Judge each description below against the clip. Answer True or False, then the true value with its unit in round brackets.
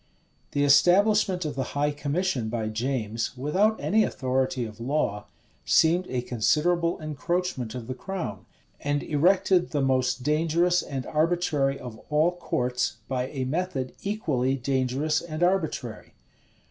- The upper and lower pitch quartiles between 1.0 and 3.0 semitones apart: False (5.4 semitones)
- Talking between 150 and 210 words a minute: False (135 wpm)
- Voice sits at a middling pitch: True (145 Hz)